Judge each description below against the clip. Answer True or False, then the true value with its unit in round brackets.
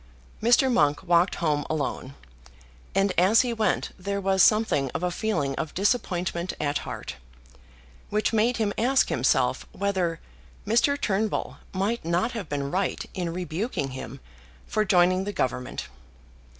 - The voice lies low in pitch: False (185 Hz)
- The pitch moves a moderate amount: True (4.6 semitones)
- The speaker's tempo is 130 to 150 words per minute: True (140 wpm)